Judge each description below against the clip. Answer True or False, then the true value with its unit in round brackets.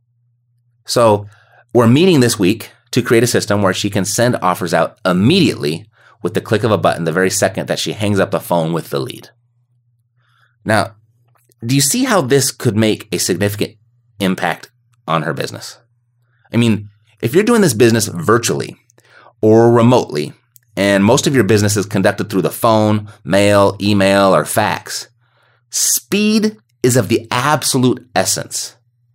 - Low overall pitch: True (115 Hz)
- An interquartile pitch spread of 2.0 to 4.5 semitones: True (3.0 semitones)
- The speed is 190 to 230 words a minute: False (160 wpm)